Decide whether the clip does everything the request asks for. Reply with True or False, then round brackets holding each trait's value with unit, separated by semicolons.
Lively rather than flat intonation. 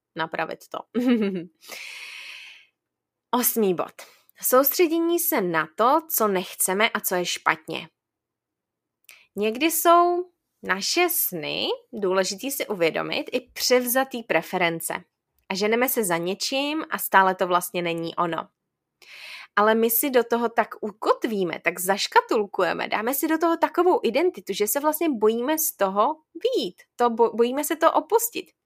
True (8.7 semitones)